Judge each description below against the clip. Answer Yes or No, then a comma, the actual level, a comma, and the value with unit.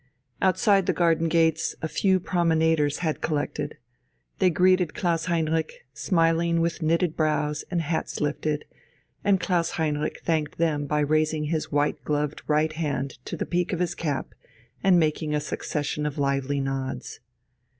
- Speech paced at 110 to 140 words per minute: No, average, 150 wpm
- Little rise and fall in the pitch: Yes, narrow, 2.2 semitones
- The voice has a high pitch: No, medium, 160 Hz